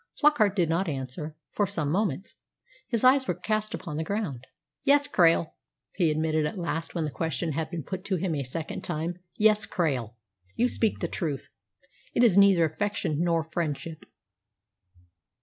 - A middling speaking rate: Yes, average, 165 wpm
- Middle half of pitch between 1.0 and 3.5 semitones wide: No, average, 4.6 semitones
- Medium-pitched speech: Yes, medium, 170 Hz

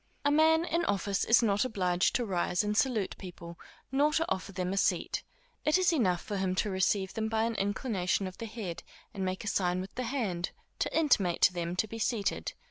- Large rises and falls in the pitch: No, average, 4.1 semitones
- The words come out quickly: Yes, fast, 215 wpm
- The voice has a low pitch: No, high, 200 Hz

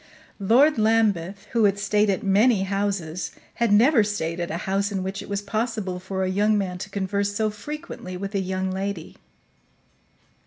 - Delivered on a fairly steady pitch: Yes, narrow, 2.1 semitones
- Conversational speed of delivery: Yes, average, 180 wpm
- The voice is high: Yes, high, 200 Hz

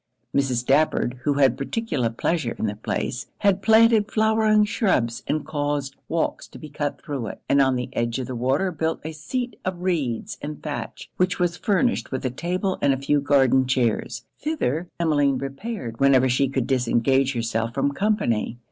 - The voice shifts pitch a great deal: Yes, wide, 5.8 semitones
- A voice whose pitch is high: No, medium, 140 Hz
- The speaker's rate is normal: Yes, average, 180 wpm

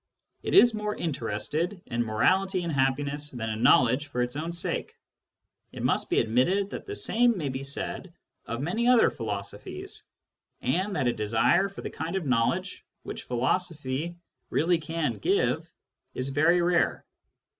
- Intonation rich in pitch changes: Yes, wide, 6.6 semitones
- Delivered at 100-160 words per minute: Yes, average, 155 wpm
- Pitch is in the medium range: Yes, medium, 150 Hz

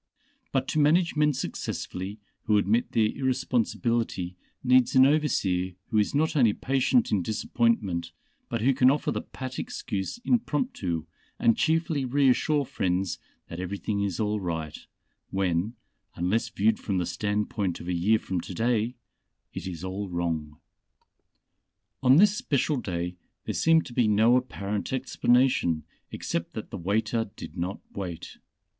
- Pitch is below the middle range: Yes, low, 110 Hz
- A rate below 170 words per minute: Yes, average, 145 wpm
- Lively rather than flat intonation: Yes, wide, 5.9 semitones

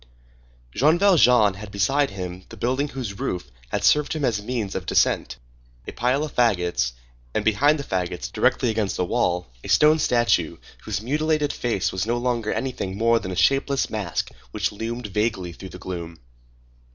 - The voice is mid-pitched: No, low, 115 Hz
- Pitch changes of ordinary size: No, wide, 6.2 semitones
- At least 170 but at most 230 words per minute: Yes, average, 175 wpm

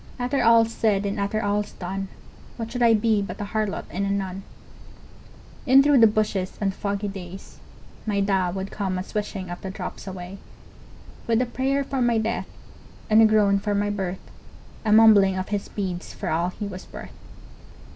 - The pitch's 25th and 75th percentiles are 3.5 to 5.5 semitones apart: No, narrow, 2.5 semitones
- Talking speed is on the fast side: No, average, 185 wpm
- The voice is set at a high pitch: Yes, high, 205 Hz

